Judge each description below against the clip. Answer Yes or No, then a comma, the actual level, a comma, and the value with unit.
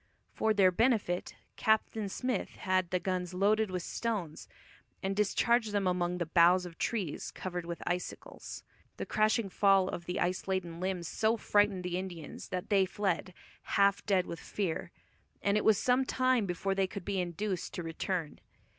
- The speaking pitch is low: No, high, 190 Hz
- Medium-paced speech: Yes, average, 165 wpm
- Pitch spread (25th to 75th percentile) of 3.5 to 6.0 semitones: No, average, 2.7 semitones